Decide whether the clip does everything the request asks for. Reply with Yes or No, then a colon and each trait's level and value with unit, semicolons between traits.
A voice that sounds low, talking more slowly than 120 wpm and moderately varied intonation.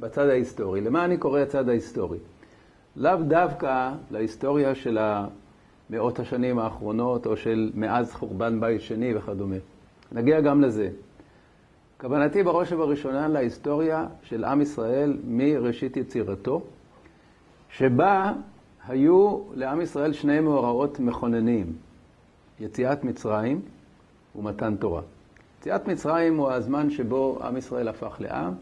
Yes: low, 125 Hz; average, 110 wpm; average, 4.8 semitones